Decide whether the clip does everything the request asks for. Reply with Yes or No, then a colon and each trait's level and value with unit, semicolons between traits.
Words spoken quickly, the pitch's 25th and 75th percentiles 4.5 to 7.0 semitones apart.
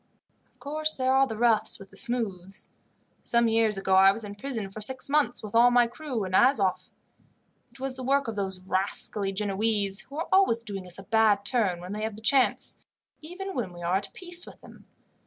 Yes: fast, 210 wpm; average, 4.9 semitones